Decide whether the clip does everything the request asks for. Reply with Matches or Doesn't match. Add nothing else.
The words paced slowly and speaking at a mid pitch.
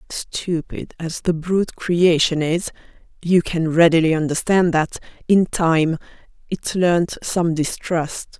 Matches